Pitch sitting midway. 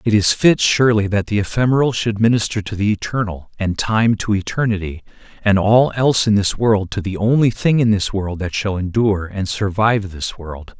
No: low, 105 Hz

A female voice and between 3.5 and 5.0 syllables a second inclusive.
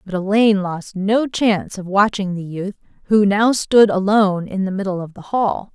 Yes: female; 4.9 syllables/s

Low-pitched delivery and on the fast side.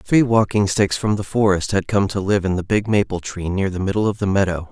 Yes: low, 100 Hz; fast, 265 wpm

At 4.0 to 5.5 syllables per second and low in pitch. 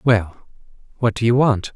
Yes: 4.4 syllables/s; low, 115 Hz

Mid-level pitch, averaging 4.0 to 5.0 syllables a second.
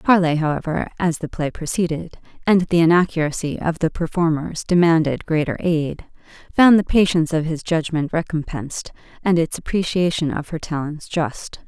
No: medium, 165 Hz; 5.2 syllables/s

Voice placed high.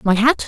Yes: high, 230 Hz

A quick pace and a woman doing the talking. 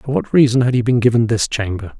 No: fast, 270 wpm; male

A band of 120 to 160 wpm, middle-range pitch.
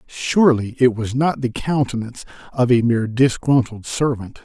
No: average, 150 wpm; low, 125 Hz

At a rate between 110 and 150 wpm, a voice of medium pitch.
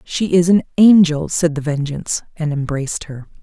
No: average, 175 wpm; medium, 160 Hz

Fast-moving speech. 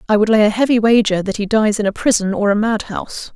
Yes: fast, 270 wpm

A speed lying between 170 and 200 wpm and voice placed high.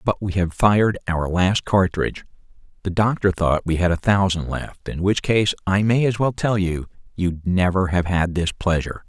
No: average, 185 wpm; very low, 95 Hz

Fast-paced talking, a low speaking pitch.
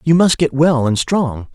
No: fast, 235 wpm; medium, 145 Hz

